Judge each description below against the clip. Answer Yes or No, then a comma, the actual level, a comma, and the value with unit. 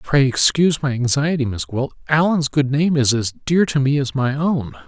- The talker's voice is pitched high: No, medium, 140 Hz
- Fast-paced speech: Yes, fast, 210 wpm